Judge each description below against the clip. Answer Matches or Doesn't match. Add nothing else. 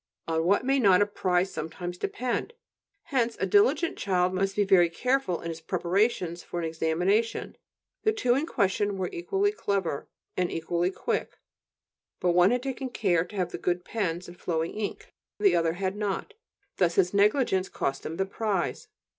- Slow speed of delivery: Doesn't match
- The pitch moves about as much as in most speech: Matches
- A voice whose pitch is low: Doesn't match